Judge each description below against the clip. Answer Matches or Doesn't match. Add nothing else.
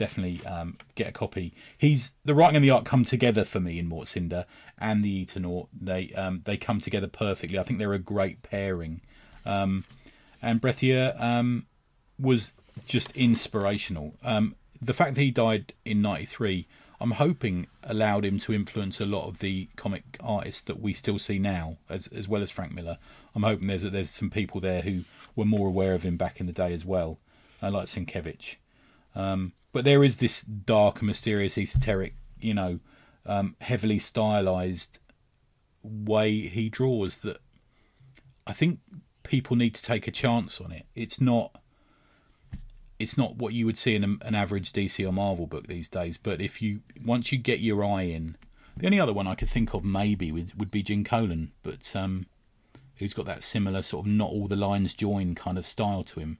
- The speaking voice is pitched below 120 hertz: Matches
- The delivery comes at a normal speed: Matches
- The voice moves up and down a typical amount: Matches